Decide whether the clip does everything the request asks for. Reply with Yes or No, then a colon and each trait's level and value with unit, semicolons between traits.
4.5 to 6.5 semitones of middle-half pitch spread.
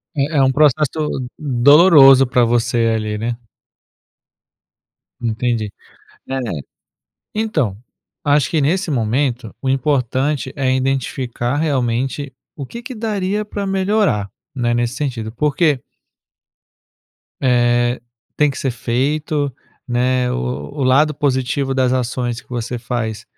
No: average, 3.5 semitones